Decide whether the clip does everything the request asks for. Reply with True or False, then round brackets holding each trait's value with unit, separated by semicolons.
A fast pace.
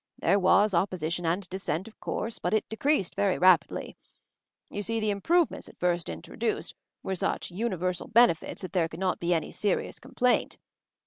True (210 wpm)